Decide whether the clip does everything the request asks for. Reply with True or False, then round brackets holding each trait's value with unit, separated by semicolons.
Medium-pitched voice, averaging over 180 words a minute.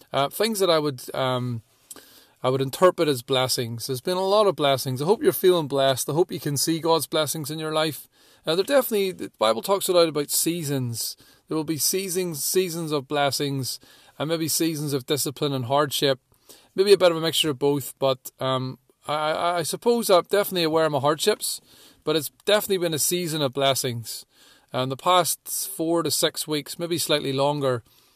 True (150 Hz; 200 wpm)